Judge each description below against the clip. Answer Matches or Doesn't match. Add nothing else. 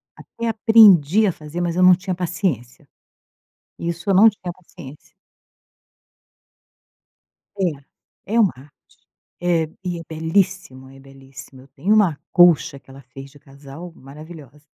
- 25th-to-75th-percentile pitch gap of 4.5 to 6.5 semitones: Matches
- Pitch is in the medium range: Matches